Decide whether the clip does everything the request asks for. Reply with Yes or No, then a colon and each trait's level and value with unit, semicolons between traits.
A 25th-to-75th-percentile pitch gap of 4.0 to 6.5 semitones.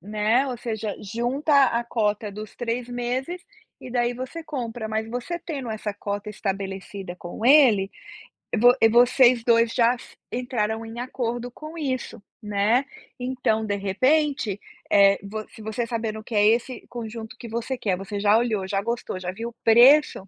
No: average, 2.9 semitones